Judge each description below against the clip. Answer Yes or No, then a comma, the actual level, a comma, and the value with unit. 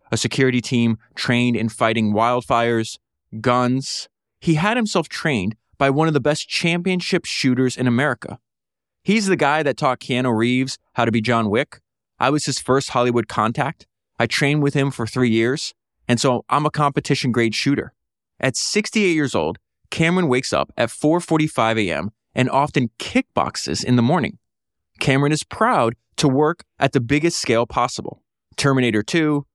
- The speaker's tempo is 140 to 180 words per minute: Yes, average, 165 wpm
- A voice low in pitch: Yes, low, 130 Hz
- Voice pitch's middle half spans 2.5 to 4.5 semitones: Yes, average, 4.1 semitones